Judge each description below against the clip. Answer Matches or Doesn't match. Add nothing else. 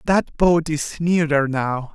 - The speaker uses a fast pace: Doesn't match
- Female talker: Doesn't match